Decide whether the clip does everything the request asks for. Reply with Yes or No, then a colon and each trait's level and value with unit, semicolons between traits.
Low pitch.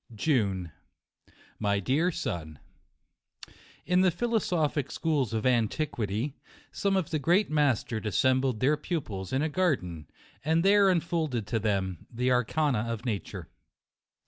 Yes: low, 130 Hz